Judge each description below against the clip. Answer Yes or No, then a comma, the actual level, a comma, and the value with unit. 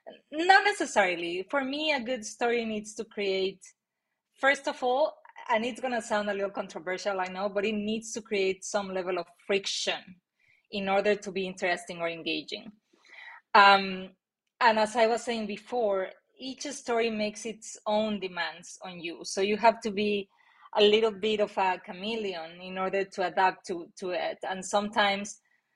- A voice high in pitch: Yes, high, 205 Hz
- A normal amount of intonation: Yes, average, 3.2 semitones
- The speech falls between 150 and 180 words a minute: Yes, average, 170 wpm